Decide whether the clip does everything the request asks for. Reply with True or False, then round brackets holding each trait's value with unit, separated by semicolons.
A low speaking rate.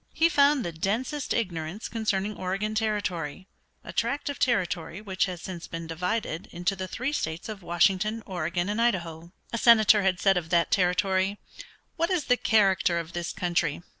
False (170 wpm)